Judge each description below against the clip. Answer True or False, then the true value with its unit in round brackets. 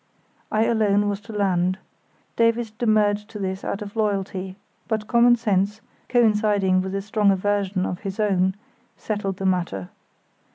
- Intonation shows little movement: True (2.2 semitones)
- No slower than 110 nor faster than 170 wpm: True (150 wpm)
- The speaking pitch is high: True (205 Hz)